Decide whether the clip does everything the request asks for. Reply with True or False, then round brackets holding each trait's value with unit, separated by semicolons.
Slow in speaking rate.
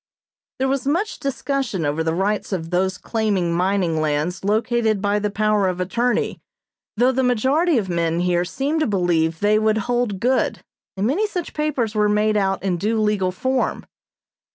False (175 wpm)